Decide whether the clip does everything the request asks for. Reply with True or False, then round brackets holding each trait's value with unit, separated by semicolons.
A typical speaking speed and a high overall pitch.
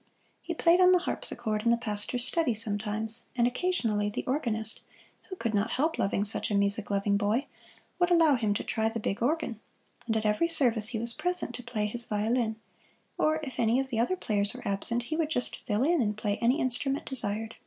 False (210 wpm; 235 Hz)